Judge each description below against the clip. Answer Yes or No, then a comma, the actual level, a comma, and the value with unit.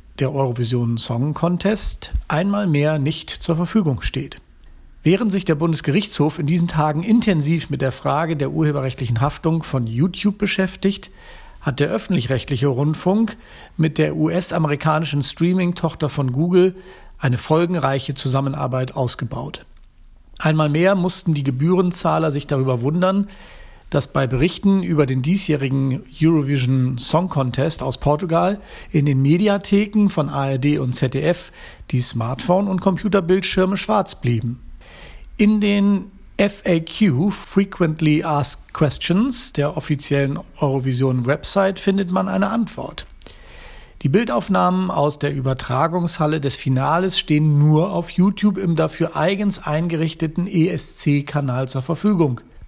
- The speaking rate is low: Yes, slow, 120 wpm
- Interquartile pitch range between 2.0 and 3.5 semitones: No, average, 5.2 semitones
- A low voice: No, medium, 155 Hz